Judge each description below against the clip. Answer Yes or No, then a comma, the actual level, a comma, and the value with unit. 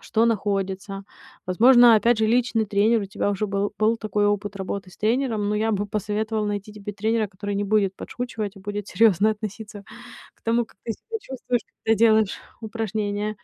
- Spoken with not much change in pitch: Yes, narrow, 1.7 semitones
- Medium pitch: No, high, 215 Hz